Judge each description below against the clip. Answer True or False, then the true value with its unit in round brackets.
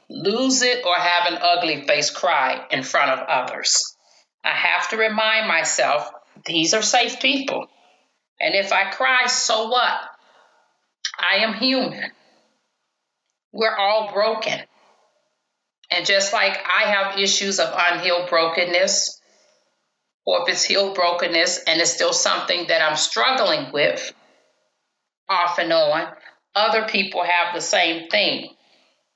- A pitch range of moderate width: False (6.3 semitones)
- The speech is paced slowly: True (130 wpm)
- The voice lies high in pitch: True (200 Hz)